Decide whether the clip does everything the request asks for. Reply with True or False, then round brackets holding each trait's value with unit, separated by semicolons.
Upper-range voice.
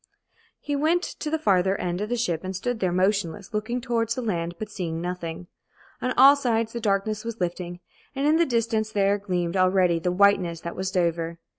True (200 Hz)